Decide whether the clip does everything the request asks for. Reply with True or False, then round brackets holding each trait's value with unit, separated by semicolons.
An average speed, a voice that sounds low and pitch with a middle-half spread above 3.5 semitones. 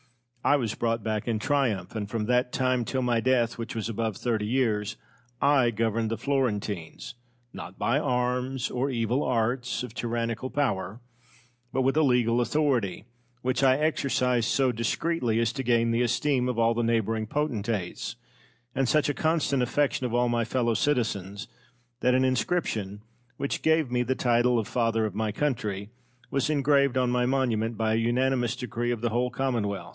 False (175 wpm; 120 Hz; 2.6 semitones)